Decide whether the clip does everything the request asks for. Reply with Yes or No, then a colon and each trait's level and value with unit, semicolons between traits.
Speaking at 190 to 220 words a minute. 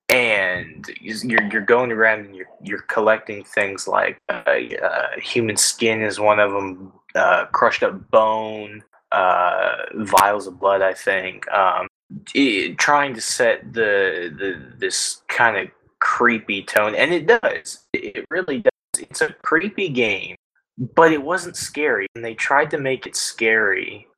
No: average, 155 wpm